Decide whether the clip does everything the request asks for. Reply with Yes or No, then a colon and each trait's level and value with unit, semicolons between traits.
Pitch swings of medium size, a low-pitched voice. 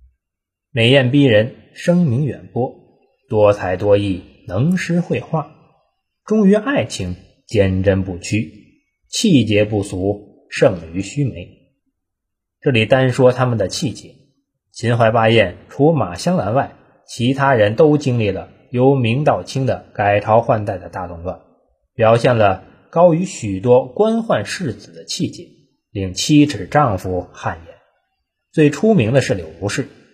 No: wide, 6.2 semitones; low, 115 Hz